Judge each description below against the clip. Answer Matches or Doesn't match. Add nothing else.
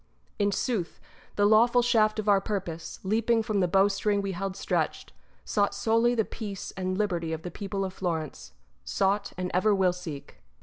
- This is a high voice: Matches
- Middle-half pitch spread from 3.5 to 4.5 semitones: Doesn't match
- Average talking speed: Matches